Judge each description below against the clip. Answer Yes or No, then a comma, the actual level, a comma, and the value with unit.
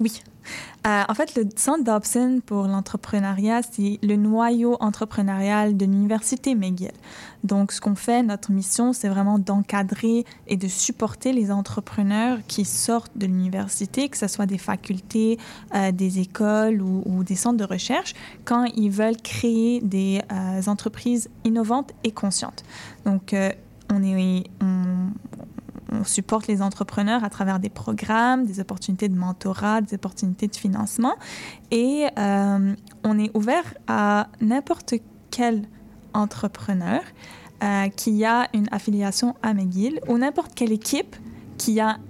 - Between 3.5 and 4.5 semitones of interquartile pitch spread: No, average, 2.7 semitones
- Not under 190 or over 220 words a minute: No, slow, 145 wpm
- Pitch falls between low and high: No, high, 210 Hz